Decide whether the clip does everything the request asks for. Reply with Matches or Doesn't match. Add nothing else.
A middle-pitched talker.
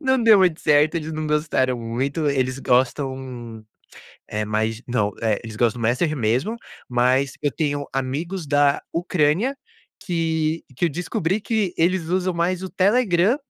Matches